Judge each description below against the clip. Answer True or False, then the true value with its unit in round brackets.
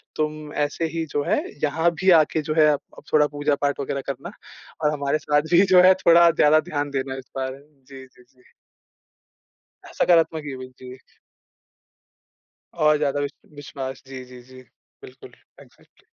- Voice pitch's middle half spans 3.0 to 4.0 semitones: False (2.4 semitones)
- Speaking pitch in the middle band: True (145 Hz)